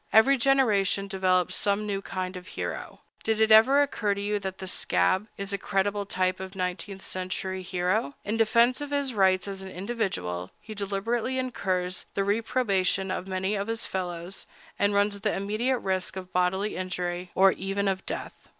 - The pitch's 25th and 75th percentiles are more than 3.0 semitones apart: No, narrow, 2.4 semitones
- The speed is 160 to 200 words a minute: Yes, average, 175 wpm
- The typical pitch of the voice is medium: No, high, 195 Hz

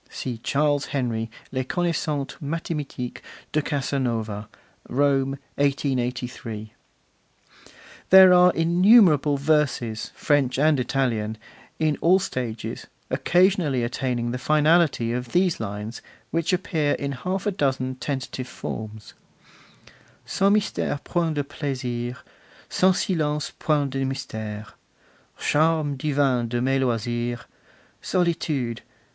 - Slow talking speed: Yes, slow, 105 wpm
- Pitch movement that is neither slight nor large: Yes, average, 4.4 semitones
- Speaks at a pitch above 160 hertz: No, medium, 140 Hz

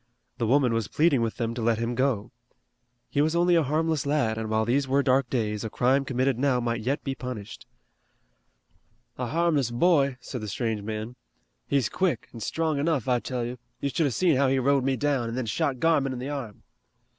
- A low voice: Yes, low, 130 Hz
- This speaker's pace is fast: Yes, fast, 215 wpm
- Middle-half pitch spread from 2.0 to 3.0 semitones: No, average, 3.4 semitones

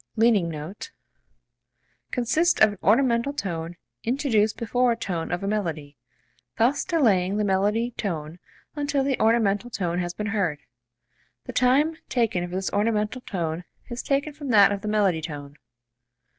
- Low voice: No, high, 210 Hz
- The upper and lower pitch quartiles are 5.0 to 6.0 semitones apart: Yes, wide, 5.5 semitones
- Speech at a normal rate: Yes, average, 150 wpm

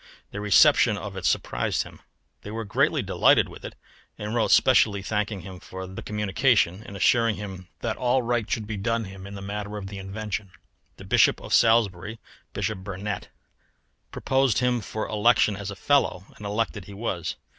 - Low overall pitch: Yes, low, 105 Hz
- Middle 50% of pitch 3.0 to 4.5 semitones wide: No, narrow, 2.6 semitones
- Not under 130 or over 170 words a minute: No, average, 180 wpm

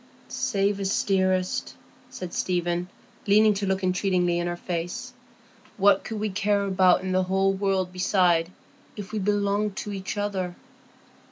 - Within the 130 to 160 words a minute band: Yes, average, 150 wpm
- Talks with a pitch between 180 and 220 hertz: Yes, high, 190 Hz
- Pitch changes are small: Yes, narrow, 1.8 semitones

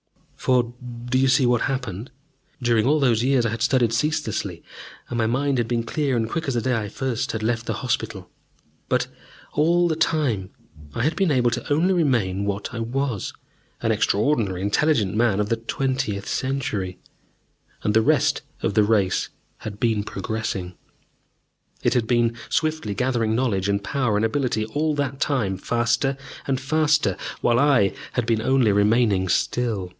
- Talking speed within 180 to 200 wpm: No, average, 170 wpm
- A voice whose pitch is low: Yes, low, 120 Hz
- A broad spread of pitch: No, average, 4.1 semitones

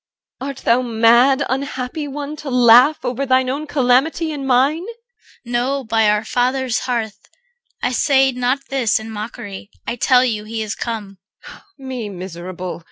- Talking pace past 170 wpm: No, average, 160 wpm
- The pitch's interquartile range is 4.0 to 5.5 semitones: No, average, 3.3 semitones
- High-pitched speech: Yes, very high, 250 Hz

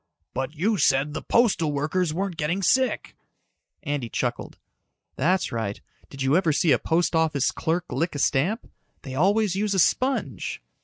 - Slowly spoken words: No, average, 160 wpm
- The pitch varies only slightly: No, average, 5.1 semitones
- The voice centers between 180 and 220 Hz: No, medium, 160 Hz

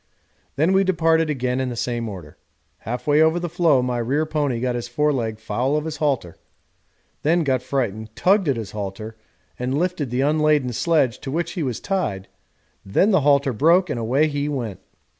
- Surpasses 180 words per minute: Yes, average, 190 wpm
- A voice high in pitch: No, medium, 140 Hz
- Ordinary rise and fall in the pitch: Yes, average, 4.8 semitones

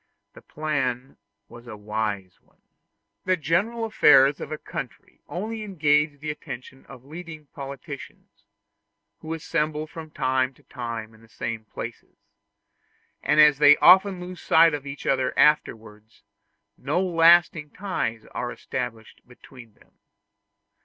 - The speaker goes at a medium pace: No, slow, 130 wpm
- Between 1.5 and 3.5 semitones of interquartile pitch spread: No, average, 5.0 semitones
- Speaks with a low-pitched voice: No, medium, 145 Hz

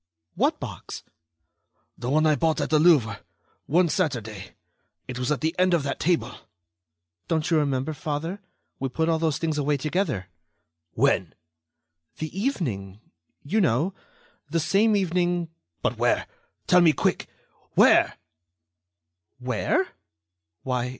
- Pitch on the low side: No, medium, 155 Hz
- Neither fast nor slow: No, slow, 130 wpm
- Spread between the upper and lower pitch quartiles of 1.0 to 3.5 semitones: No, average, 4.4 semitones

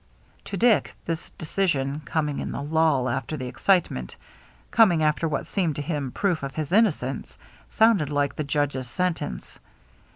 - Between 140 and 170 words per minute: Yes, average, 155 wpm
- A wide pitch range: No, average, 4.3 semitones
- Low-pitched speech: No, medium, 150 Hz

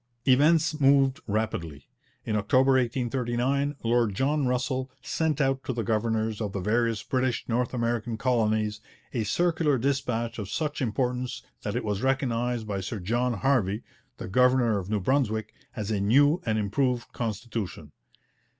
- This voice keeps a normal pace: Yes, average, 150 wpm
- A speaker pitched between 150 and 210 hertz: No, low, 120 Hz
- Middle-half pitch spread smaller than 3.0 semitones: No, average, 3.5 semitones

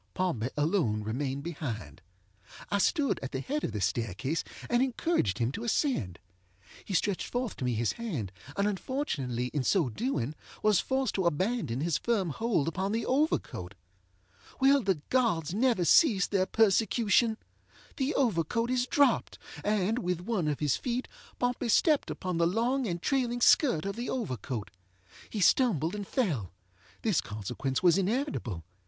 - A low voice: No, high, 190 Hz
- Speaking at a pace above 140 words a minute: Yes, average, 155 wpm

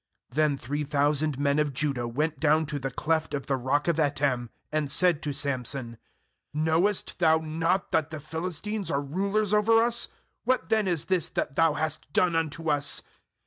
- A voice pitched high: No, medium, 155 Hz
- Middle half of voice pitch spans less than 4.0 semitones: Yes, average, 2.7 semitones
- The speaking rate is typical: Yes, average, 180 wpm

